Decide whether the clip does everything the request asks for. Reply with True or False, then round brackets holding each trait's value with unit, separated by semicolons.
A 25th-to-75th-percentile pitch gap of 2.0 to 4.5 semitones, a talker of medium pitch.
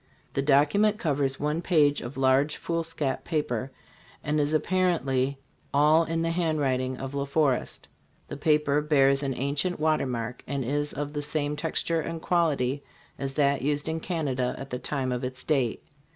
True (2.7 semitones; 145 Hz)